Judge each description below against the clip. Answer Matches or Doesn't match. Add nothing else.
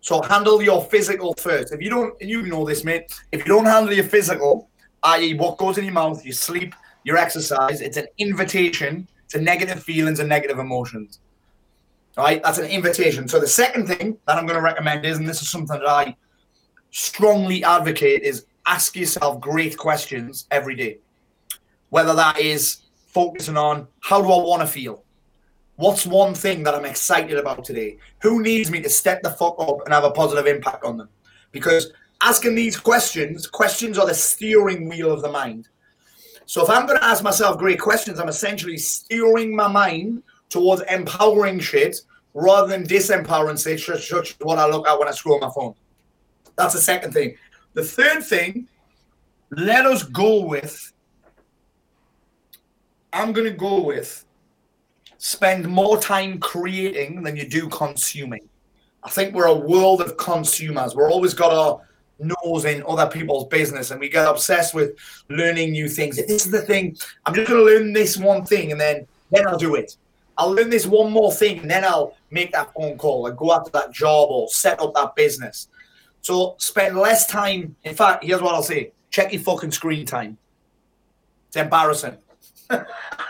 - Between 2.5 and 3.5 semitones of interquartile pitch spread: Doesn't match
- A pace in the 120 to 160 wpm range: Doesn't match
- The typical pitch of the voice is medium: Matches